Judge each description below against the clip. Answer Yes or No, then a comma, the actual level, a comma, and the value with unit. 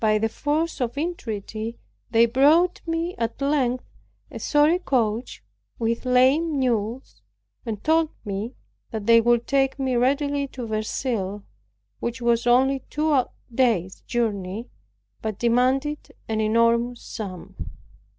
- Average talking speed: No, slow, 125 wpm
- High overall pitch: Yes, high, 240 Hz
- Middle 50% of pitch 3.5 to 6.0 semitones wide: Yes, average, 3.8 semitones